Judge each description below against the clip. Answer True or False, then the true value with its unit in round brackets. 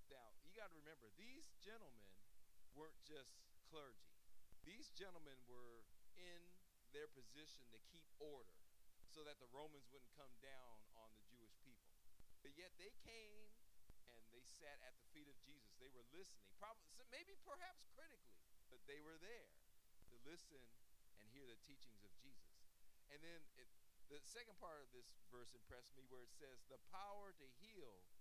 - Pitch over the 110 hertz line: True (135 Hz)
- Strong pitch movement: True (6.3 semitones)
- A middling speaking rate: True (170 wpm)